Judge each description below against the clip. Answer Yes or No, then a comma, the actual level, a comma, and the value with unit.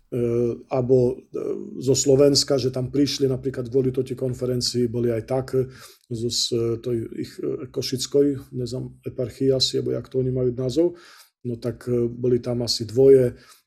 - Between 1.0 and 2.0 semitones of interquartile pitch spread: Yes, narrow, 1.6 semitones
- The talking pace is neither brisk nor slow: Yes, average, 135 wpm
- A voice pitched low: Yes, low, 125 Hz